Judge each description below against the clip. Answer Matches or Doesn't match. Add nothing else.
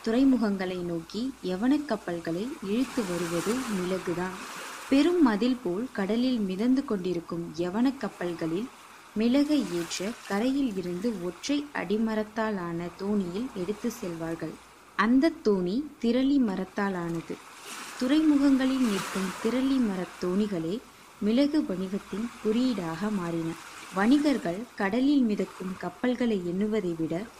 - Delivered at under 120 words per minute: Matches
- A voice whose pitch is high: Matches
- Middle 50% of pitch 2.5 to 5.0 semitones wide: Doesn't match